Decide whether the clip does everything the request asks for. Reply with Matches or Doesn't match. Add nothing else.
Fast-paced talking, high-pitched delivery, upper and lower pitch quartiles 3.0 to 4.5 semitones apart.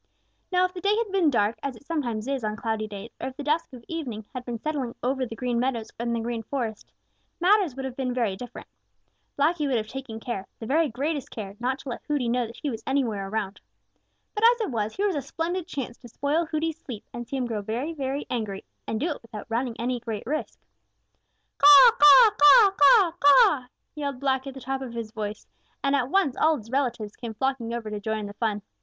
Doesn't match